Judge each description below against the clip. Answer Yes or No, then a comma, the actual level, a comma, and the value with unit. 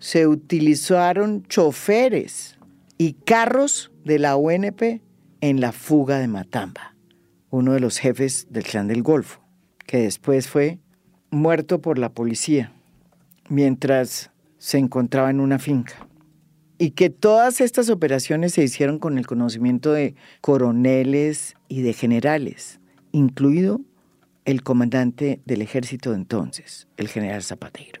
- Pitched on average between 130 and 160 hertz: Yes, medium, 140 Hz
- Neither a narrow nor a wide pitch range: Yes, average, 4.6 semitones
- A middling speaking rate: No, slow, 125 wpm